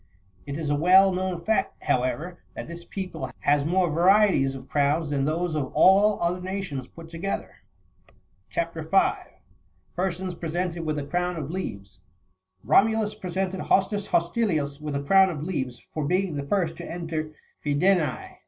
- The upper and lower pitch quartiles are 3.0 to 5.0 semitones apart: Yes, average, 4.3 semitones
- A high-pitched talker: No, medium, 170 Hz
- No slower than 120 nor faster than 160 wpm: Yes, average, 155 wpm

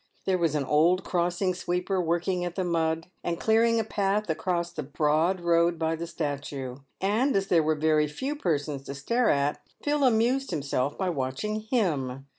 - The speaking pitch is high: No, medium, 170 Hz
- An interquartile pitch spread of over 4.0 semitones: Yes, average, 4.4 semitones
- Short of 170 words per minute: No, average, 180 wpm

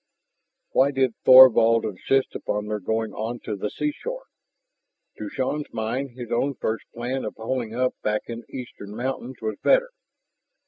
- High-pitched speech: No, low, 120 Hz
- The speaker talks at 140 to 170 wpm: Yes, average, 155 wpm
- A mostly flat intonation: No, average, 3.2 semitones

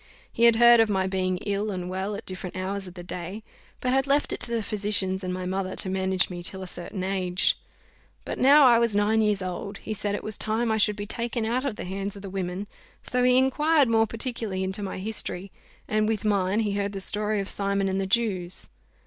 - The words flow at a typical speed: No, fast, 235 wpm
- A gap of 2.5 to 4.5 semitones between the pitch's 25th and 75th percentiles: Yes, average, 2.9 semitones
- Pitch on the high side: Yes, high, 200 Hz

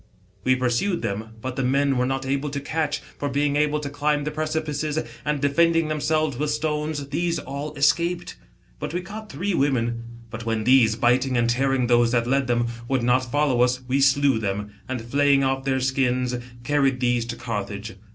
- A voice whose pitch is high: No, low, 135 Hz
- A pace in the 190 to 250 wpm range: Yes, average, 195 wpm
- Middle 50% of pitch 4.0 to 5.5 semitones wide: No, average, 3.3 semitones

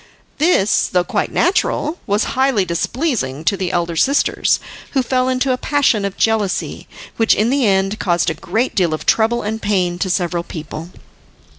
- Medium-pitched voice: No, high, 205 Hz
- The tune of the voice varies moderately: No, wide, 6.3 semitones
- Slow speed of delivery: No, average, 170 wpm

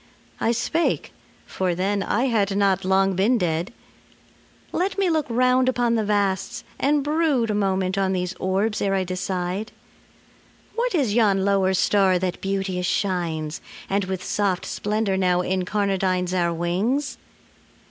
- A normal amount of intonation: Yes, average, 3.4 semitones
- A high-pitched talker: Yes, high, 195 Hz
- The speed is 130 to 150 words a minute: Yes, average, 145 wpm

